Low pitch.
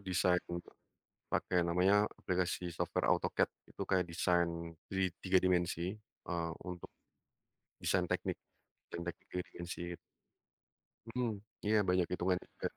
Yes: very low, 90 Hz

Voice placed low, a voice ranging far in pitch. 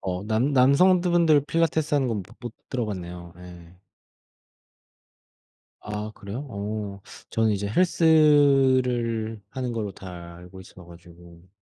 Yes: low, 110 Hz; wide, 7.0 semitones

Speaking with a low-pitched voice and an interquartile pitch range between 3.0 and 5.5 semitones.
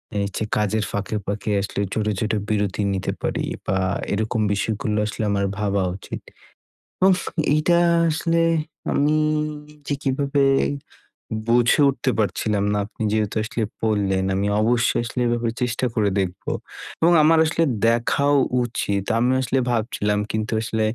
Yes: low, 110 Hz; average, 3.9 semitones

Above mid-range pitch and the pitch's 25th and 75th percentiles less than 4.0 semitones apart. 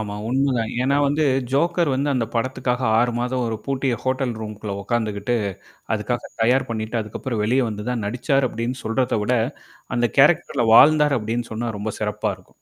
No: low, 120 Hz; average, 3.3 semitones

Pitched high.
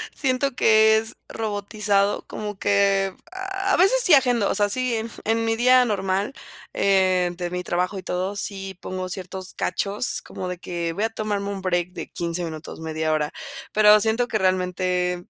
Yes: high, 200 Hz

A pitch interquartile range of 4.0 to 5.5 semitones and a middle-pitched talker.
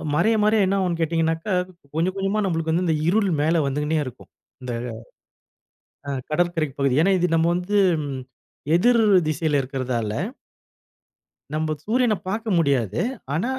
Yes: average, 4.7 semitones; medium, 165 Hz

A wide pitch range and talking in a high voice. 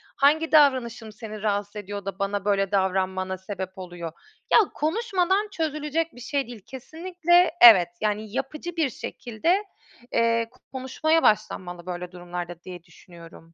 Yes: wide, 8.3 semitones; high, 215 Hz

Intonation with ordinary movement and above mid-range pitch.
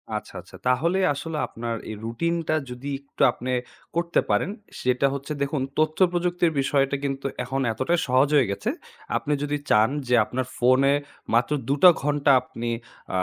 No: average, 3.9 semitones; medium, 140 Hz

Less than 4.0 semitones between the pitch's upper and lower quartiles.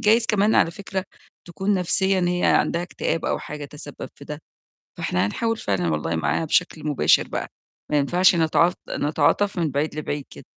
No: average, 4.7 semitones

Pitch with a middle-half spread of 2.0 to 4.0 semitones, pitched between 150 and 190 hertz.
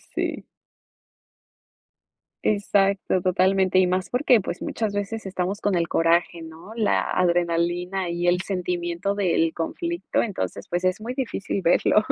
Yes: narrow, 2.6 semitones; medium, 185 Hz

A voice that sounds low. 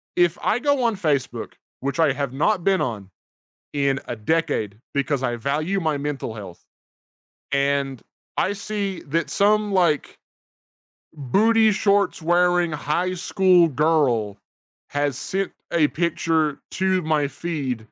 No: medium, 155 Hz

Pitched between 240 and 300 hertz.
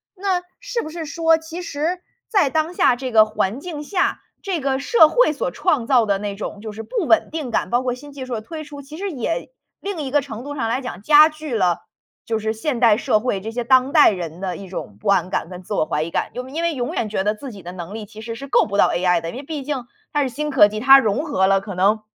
Yes: very high, 255 Hz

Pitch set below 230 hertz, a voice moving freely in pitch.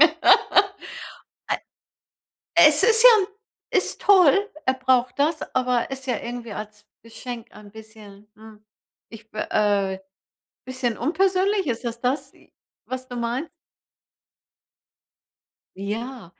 No: high, 245 Hz; wide, 5.7 semitones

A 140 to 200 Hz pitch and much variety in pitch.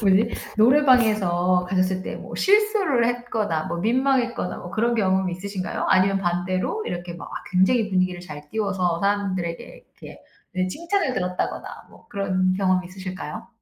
No: high, 190 Hz; average, 4.2 semitones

